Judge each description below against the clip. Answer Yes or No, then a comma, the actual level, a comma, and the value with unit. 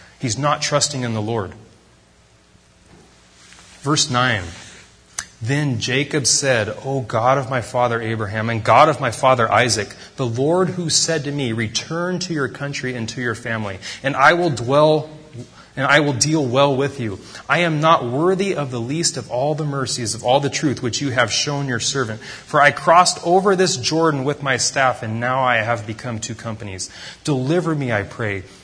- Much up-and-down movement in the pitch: No, average, 4.5 semitones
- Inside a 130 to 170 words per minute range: No, average, 185 wpm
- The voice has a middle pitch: No, low, 130 Hz